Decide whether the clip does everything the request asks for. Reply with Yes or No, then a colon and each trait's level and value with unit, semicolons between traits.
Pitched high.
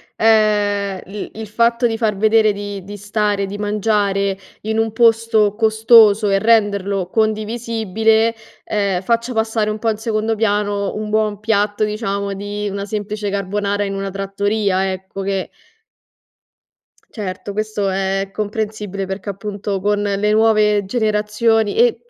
Yes: high, 210 Hz